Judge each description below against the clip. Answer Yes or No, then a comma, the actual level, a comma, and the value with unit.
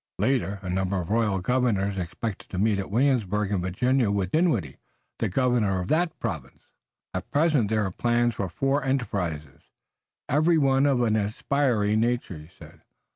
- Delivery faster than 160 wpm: Yes, average, 170 wpm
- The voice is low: Yes, low, 110 Hz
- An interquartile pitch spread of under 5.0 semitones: No, average, 5.3 semitones